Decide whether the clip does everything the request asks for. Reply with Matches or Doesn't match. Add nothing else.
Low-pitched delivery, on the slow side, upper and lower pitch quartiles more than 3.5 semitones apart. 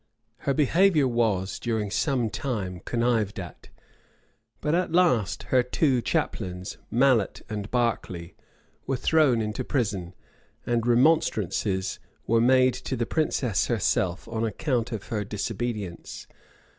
Matches